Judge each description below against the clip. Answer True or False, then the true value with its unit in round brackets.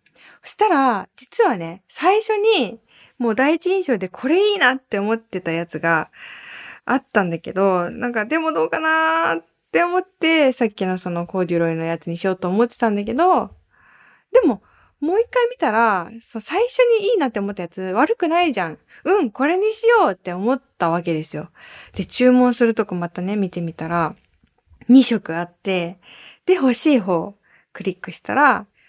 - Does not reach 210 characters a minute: False (330 characters per minute)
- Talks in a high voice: True (225 Hz)